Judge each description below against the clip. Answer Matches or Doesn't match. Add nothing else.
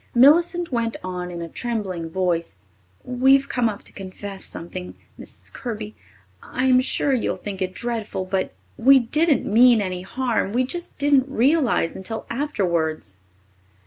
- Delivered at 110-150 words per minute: Matches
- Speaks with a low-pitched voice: Doesn't match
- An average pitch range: Doesn't match